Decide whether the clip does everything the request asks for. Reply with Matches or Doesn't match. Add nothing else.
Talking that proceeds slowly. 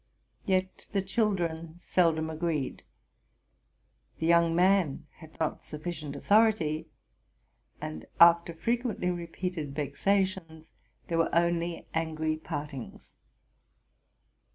Matches